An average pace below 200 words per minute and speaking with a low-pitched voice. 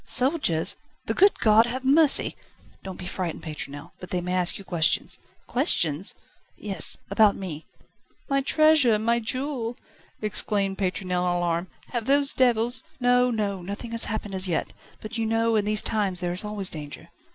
No: average, 170 wpm; high, 210 Hz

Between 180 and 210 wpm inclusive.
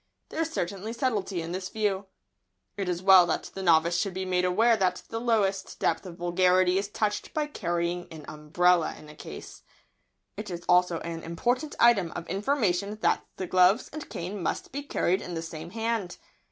Yes: average, 190 wpm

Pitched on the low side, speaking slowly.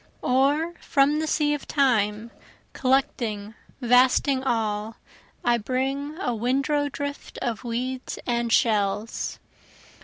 No: very high, 255 Hz; slow, 110 wpm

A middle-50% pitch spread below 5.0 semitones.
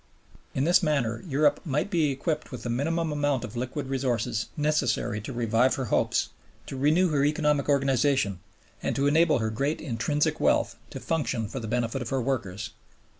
Yes: average, 3.9 semitones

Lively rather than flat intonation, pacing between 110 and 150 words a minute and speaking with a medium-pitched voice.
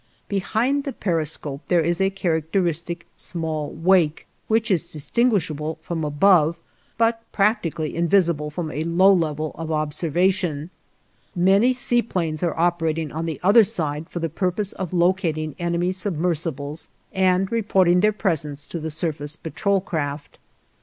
No: average, 3.5 semitones; average, 140 wpm; medium, 170 Hz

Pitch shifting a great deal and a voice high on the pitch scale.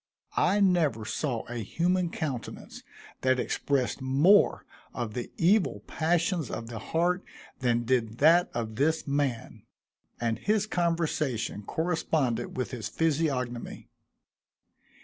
No: wide, 5.9 semitones; medium, 140 Hz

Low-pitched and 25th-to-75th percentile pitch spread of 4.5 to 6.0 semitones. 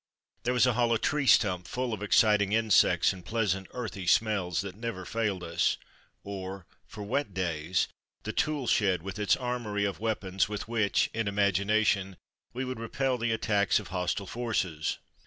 No: low, 105 Hz; average, 3.3 semitones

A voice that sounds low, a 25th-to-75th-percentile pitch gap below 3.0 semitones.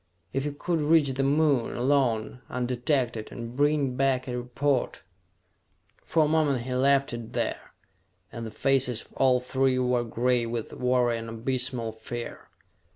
Yes: low, 125 Hz; narrow, 2.4 semitones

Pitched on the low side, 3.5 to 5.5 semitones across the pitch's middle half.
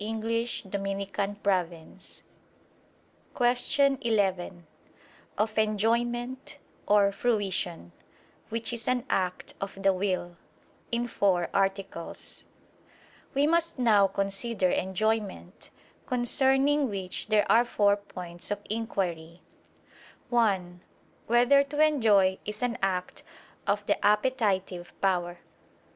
No: high, 205 Hz; average, 4.1 semitones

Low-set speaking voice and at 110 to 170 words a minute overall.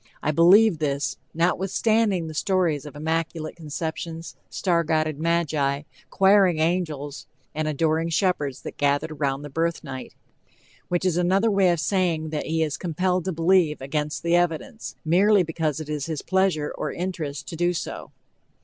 No: medium, 165 Hz; average, 160 wpm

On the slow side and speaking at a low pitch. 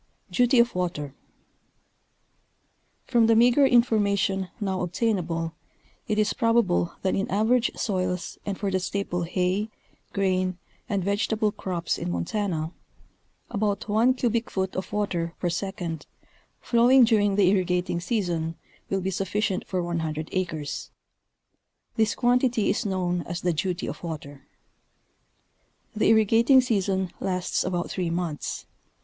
No: slow, 130 wpm; high, 190 Hz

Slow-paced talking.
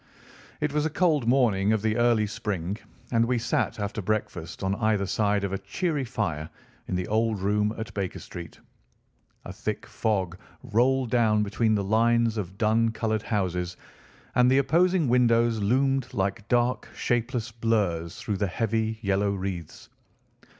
No: average, 155 wpm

